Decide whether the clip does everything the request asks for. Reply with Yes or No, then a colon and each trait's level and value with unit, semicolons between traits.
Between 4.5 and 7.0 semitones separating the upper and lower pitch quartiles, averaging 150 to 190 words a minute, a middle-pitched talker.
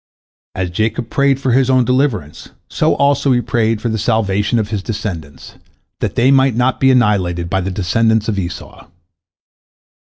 No: average, 4.8 semitones; average, 165 wpm; low, 110 Hz